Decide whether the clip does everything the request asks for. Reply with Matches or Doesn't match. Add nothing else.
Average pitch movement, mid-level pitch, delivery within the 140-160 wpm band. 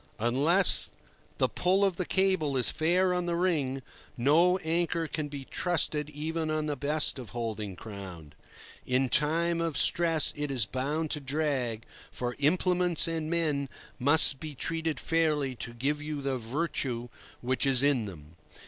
Matches